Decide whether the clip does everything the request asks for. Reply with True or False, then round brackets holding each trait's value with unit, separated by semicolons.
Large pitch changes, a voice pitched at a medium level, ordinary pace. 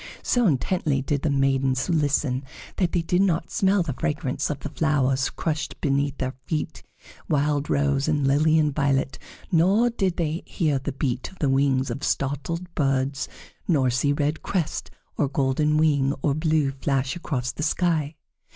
False (2.8 semitones; 145 Hz; 165 wpm)